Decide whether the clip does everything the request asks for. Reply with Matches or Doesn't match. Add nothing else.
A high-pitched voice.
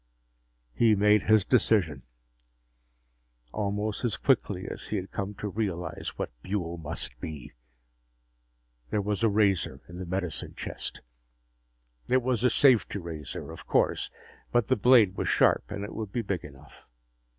Doesn't match